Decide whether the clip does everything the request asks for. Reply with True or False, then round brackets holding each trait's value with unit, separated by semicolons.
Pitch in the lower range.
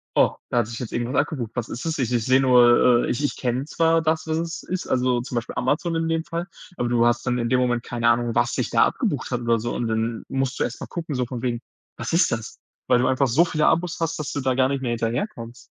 True (125 Hz)